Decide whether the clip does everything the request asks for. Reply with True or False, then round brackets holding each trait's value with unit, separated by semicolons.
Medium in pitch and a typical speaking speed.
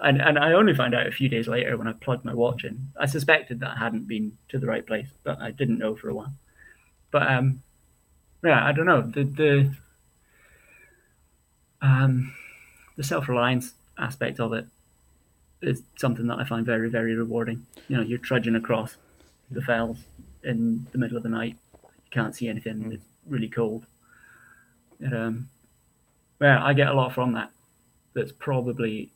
False (120 Hz; 180 wpm)